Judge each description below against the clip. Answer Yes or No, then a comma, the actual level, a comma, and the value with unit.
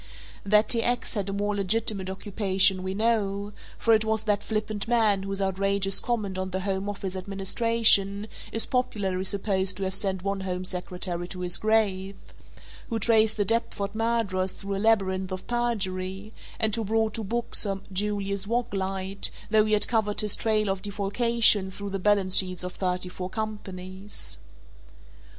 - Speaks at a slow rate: No, average, 165 wpm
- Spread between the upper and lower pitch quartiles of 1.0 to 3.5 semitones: Yes, narrow, 2.4 semitones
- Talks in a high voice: Yes, high, 200 Hz